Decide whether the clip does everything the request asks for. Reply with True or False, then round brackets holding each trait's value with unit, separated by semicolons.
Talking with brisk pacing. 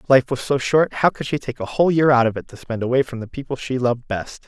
True (310 wpm)